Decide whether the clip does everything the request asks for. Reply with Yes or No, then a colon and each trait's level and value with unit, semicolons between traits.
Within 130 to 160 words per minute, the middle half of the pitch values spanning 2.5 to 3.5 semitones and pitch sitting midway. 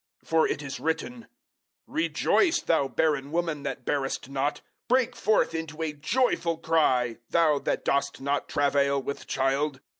Yes: average, 150 wpm; average, 2.9 semitones; medium, 150 Hz